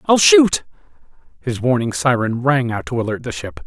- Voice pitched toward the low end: Yes, low, 120 Hz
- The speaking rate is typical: Yes, average, 180 wpm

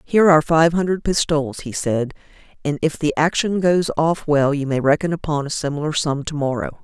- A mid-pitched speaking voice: Yes, medium, 155 Hz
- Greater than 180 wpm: Yes, average, 200 wpm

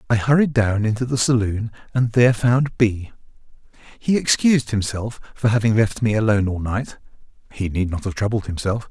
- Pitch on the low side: Yes, low, 110 Hz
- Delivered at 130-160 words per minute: No, average, 170 wpm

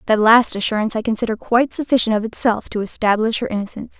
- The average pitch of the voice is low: No, high, 225 Hz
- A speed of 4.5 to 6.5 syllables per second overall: No, 7.1 syllables/s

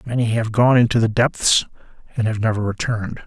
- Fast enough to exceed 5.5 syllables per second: Yes, 5.7 syllables/s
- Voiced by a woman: No, male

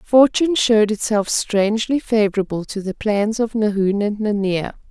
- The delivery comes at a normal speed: Yes, average, 145 wpm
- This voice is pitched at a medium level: No, high, 215 Hz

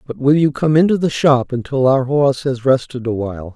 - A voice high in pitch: No, low, 135 Hz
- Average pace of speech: No, fast, 220 wpm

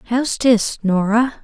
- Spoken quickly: No, slow, 125 wpm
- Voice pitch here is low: No, high, 225 Hz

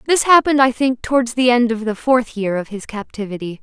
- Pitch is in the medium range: No, high, 240 Hz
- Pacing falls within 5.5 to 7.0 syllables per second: Yes, 5.8 syllables/s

